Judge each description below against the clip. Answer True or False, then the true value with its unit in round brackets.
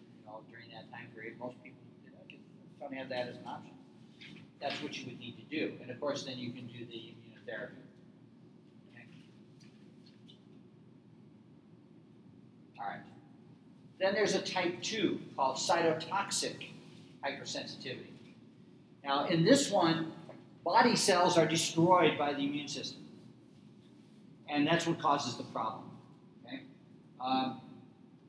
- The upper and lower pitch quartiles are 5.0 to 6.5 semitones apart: True (5.6 semitones)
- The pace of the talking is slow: True (130 wpm)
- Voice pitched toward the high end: False (155 Hz)